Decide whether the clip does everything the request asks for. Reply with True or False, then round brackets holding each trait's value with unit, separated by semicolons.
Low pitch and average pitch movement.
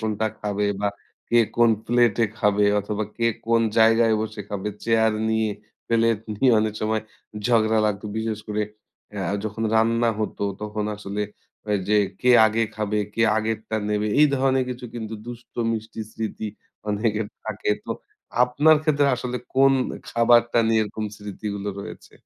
False (110 Hz; 1.8 semitones)